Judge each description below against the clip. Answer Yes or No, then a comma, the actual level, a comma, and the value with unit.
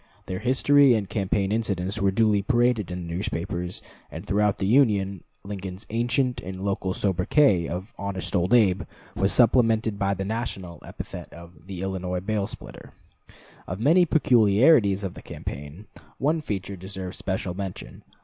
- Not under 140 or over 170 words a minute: Yes, average, 155 wpm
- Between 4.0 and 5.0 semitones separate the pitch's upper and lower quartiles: No, average, 3.4 semitones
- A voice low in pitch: Yes, low, 100 Hz